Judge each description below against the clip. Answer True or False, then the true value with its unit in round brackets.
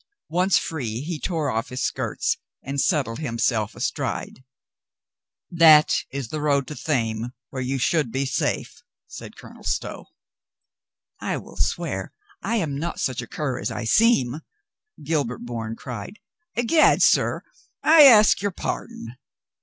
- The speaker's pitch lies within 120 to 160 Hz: True (140 Hz)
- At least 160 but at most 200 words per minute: False (145 wpm)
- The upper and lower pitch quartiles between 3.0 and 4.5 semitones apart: False (5.5 semitones)